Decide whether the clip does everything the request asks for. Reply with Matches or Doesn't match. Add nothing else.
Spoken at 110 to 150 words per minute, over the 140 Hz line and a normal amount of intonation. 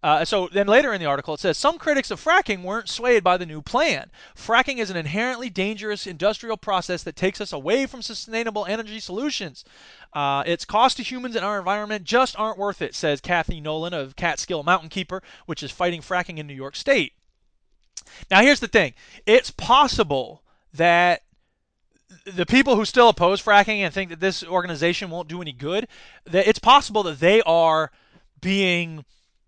Doesn't match